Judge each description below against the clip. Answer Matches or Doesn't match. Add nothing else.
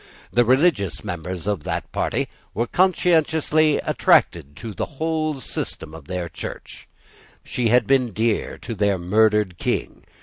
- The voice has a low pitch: Matches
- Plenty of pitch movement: Matches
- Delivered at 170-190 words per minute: Doesn't match